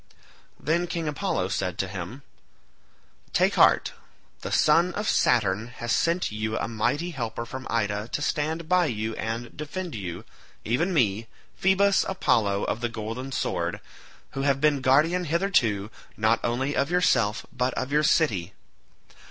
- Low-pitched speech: Yes, low, 125 Hz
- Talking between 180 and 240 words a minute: No, average, 150 wpm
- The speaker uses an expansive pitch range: Yes, wide, 6.6 semitones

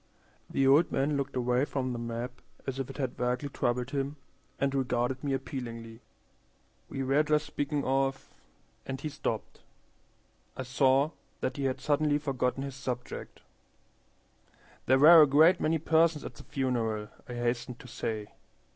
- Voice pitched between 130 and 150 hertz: Yes, low, 135 Hz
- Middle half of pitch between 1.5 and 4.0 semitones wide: Yes, narrow, 2.5 semitones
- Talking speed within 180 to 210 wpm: No, average, 155 wpm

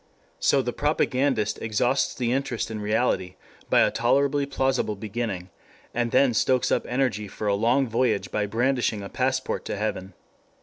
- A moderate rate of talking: Yes, average, 160 wpm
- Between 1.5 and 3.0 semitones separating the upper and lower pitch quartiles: No, average, 3.7 semitones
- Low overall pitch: Yes, low, 120 Hz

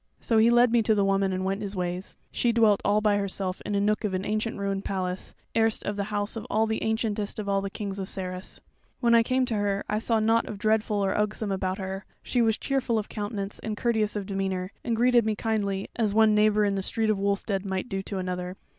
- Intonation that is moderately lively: No, narrow, 2.1 semitones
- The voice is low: No, high, 205 Hz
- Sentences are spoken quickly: Yes, fast, 235 wpm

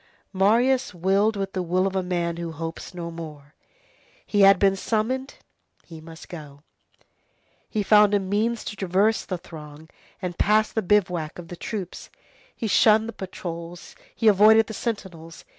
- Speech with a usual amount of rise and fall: Yes, average, 3.9 semitones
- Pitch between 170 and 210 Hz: Yes, high, 190 Hz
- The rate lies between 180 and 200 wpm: No, average, 165 wpm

